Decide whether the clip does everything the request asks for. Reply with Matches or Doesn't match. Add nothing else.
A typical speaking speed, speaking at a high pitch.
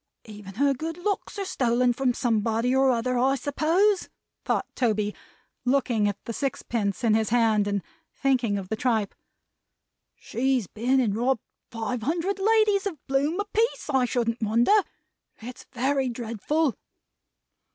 Matches